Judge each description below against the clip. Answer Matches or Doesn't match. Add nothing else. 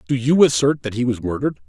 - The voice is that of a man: Matches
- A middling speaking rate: Doesn't match